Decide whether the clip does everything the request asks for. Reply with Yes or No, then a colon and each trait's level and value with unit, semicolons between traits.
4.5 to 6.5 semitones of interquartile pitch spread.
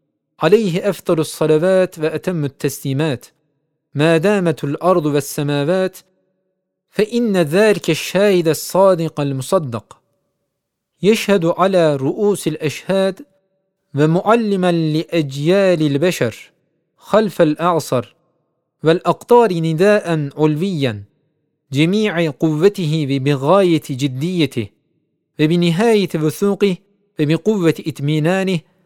No: average, 3.7 semitones